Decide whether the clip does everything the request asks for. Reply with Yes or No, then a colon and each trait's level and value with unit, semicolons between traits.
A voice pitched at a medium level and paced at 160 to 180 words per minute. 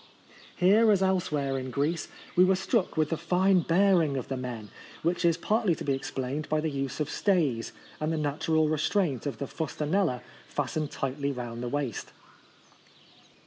Yes: medium, 155 Hz; average, 170 wpm